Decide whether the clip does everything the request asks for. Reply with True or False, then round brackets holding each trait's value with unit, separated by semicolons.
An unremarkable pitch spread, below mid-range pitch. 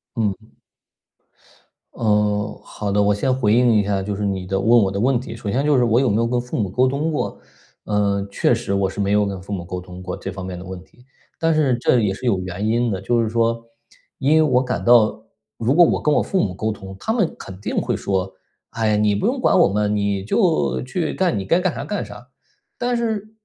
True (4.1 semitones; 105 Hz)